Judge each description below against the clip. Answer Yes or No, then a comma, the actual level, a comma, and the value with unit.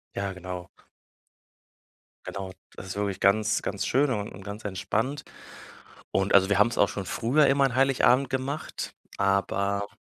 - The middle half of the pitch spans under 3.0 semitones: No, average, 4.8 semitones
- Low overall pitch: Yes, low, 100 Hz